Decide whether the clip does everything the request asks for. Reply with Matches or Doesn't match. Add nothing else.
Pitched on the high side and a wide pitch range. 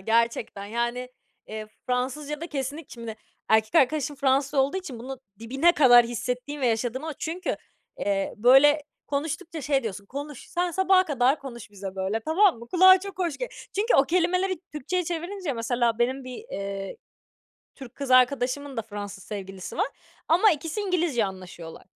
Matches